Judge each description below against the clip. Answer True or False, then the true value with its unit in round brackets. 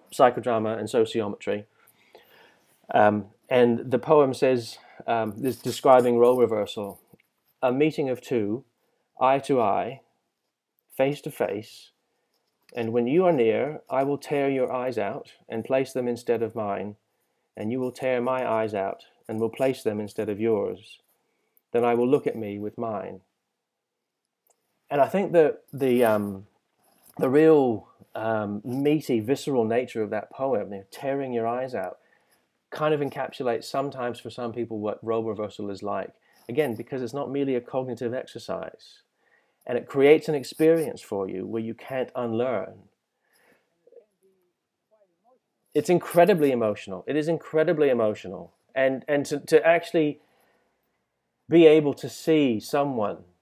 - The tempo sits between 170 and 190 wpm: False (150 wpm)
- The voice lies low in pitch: True (125 Hz)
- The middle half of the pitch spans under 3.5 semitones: False (4.1 semitones)